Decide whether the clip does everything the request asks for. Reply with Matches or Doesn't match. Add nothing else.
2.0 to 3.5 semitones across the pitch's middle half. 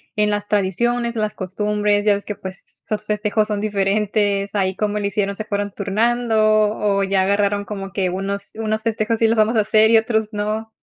Doesn't match